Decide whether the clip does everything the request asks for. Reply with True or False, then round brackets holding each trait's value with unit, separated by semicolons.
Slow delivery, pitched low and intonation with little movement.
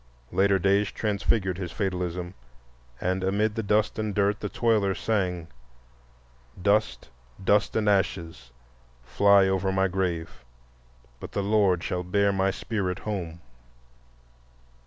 True (120 wpm; 95 Hz; 2.2 semitones)